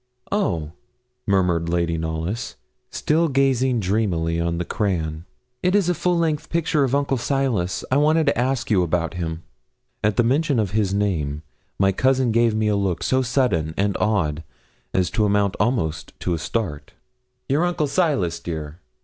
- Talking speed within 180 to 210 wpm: No, average, 165 wpm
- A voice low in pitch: Yes, low, 105 Hz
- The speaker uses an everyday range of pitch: No, wide, 8.0 semitones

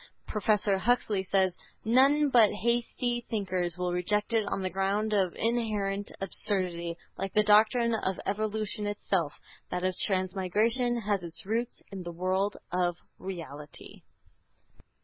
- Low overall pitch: No, high, 200 Hz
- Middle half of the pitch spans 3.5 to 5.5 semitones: No, average, 2.9 semitones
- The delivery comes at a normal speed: No, slow, 130 wpm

